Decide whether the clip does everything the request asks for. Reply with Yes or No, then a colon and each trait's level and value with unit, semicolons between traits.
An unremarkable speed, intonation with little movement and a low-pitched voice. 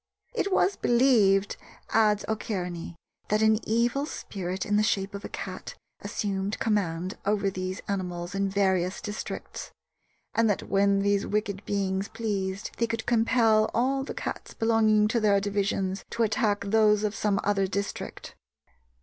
No: average, 150 wpm; narrow, 2.2 semitones; high, 205 Hz